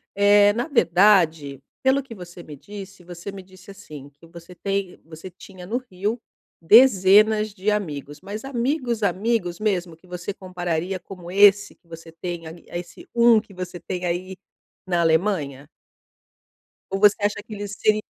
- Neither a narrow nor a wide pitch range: Yes, average, 3.4 semitones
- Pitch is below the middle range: No, high, 190 Hz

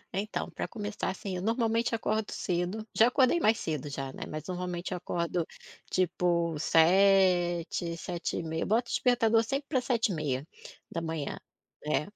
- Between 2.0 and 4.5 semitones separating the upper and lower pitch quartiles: No, average, 4.9 semitones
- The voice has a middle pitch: Yes, medium, 180 Hz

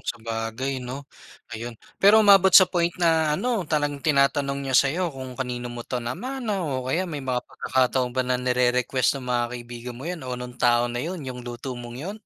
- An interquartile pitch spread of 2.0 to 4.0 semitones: No, average, 4.5 semitones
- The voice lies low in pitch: Yes, low, 130 Hz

